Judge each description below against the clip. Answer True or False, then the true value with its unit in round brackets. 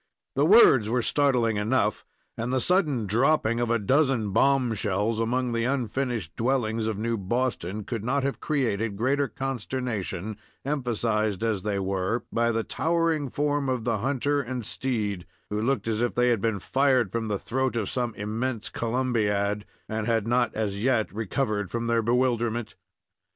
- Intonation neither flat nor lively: True (3.5 semitones)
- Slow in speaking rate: False (160 wpm)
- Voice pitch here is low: True (115 Hz)